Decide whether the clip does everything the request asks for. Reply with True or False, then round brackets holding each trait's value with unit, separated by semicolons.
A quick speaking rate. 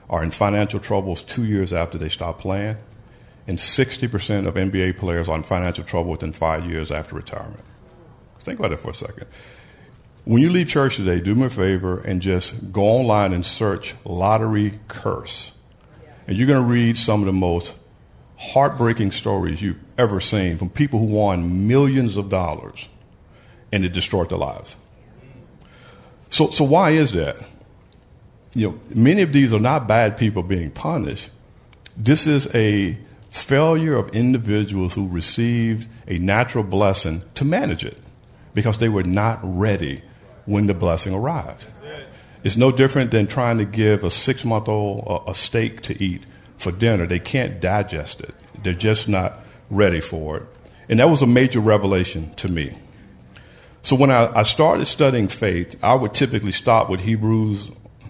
False (165 wpm)